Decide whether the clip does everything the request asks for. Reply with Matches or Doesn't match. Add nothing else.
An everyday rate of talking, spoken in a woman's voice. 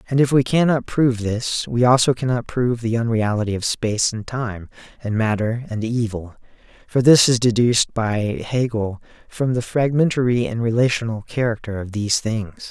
Doesn't match